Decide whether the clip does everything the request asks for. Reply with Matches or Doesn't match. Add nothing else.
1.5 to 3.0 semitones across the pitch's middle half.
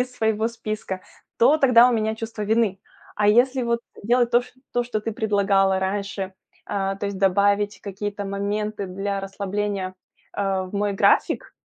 Matches